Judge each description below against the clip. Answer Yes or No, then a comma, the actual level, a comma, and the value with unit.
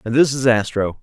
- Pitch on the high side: No, low, 120 Hz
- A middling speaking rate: No, fast, 235 wpm